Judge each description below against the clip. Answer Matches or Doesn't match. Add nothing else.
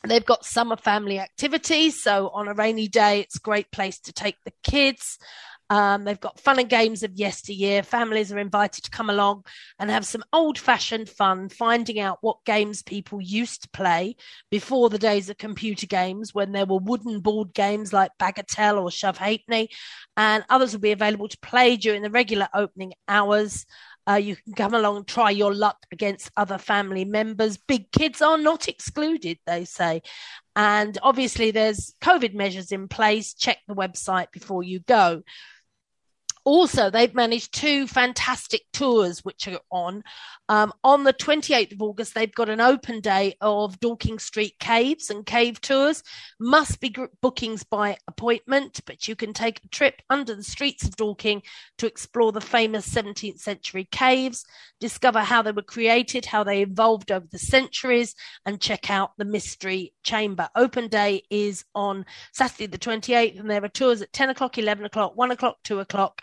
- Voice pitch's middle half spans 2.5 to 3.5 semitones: Matches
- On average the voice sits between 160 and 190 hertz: Doesn't match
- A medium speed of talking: Matches